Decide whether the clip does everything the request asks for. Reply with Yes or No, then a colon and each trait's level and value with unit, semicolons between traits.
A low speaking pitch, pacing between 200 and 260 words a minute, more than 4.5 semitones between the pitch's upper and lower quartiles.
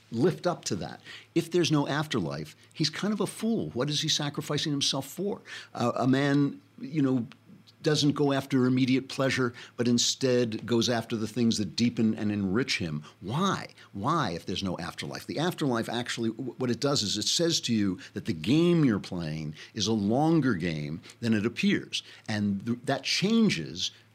No: low, 125 Hz; average, 185 wpm; average, 5.3 semitones